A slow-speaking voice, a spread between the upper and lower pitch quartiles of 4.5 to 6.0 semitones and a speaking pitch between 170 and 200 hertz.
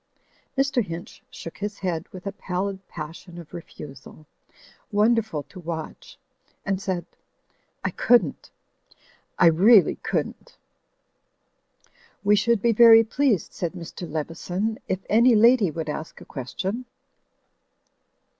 Yes: slow, 115 wpm; average, 4.8 semitones; high, 190 Hz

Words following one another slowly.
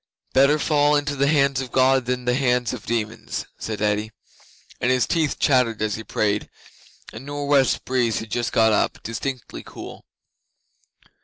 No: average, 165 wpm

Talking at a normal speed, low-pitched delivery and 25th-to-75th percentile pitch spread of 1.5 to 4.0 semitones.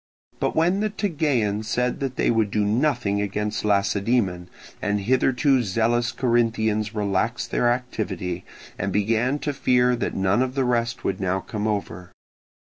Yes: average, 150 wpm; low, 115 Hz; average, 3.5 semitones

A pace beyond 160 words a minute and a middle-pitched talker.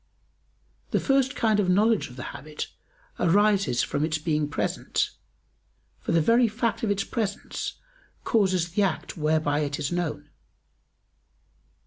No: slow, 135 wpm; medium, 180 Hz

